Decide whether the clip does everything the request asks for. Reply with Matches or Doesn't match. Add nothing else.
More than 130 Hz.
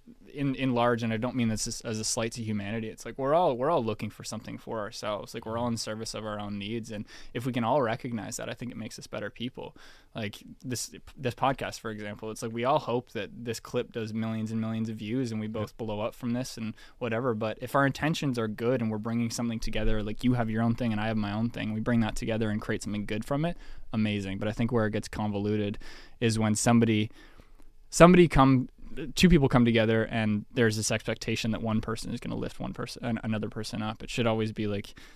Doesn't match